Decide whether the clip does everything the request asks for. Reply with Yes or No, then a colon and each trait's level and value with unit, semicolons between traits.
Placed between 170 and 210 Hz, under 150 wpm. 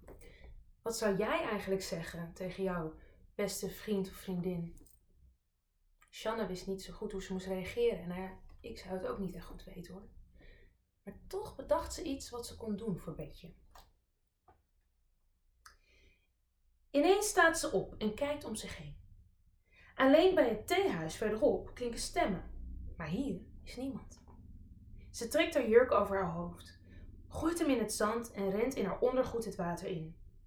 No: high, 190 Hz; average, 165 wpm